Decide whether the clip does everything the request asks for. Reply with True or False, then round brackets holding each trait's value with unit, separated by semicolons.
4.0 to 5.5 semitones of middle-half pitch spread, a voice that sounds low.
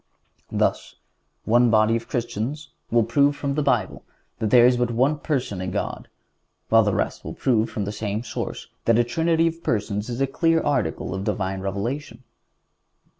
True (4.5 semitones; 120 Hz)